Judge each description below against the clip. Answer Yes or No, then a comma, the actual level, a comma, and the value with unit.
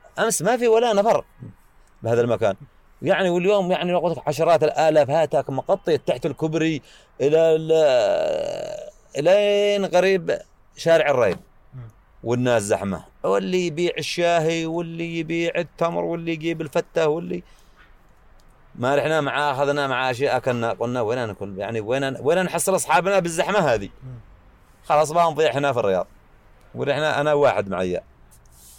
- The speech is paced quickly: No, average, 125 wpm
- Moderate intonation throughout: No, wide, 5.7 semitones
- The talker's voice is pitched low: No, medium, 155 Hz